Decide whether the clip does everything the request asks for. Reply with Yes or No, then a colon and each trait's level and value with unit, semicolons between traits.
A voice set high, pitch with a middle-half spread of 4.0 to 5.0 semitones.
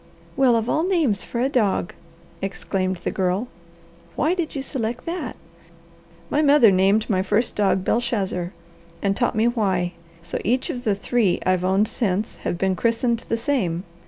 Yes: high, 220 Hz; average, 4.6 semitones